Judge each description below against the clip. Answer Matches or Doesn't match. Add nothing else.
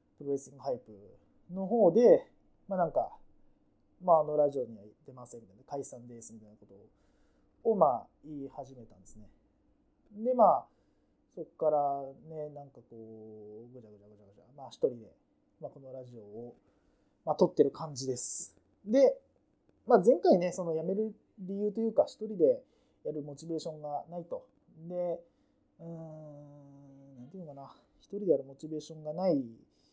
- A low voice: Doesn't match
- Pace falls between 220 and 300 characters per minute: Doesn't match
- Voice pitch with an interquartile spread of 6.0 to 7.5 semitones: Matches